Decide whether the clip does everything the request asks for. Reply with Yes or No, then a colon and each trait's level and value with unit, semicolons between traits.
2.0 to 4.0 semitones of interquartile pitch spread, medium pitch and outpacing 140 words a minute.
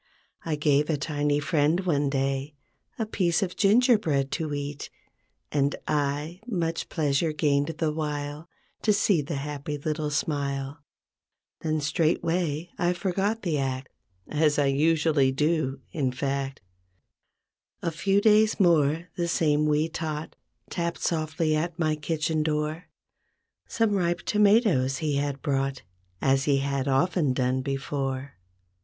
No: average, 3.2 semitones; medium, 150 Hz; slow, 135 wpm